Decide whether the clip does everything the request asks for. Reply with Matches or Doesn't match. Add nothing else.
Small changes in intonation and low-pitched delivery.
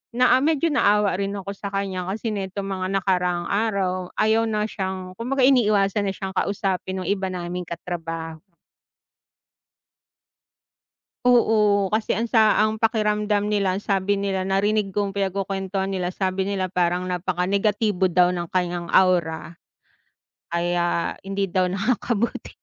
Doesn't match